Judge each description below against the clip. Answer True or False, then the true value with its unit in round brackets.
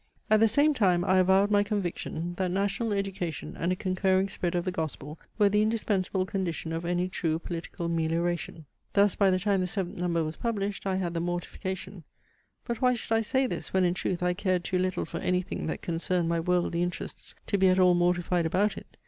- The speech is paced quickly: True (215 wpm)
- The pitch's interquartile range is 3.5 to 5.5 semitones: False (2.4 semitones)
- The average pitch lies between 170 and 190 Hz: True (185 Hz)